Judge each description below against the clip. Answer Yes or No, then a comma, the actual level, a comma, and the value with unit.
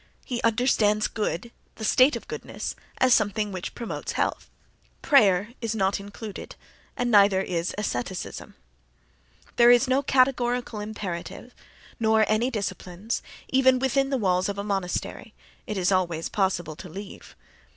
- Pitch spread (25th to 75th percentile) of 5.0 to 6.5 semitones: No, average, 4.1 semitones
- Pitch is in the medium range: No, high, 210 Hz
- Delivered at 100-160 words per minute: Yes, average, 140 wpm